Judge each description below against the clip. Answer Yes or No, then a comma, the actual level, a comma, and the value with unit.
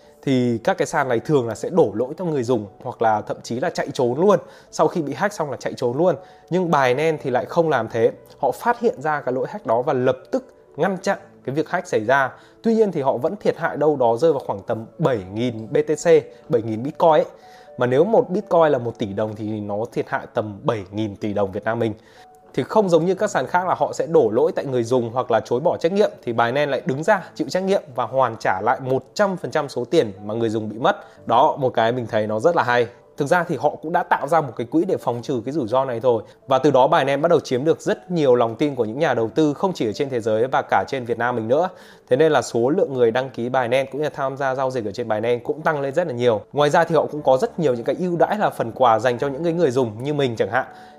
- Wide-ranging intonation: Yes, wide, 6.1 semitones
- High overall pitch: No, low, 135 Hz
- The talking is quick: Yes, fast, 290 wpm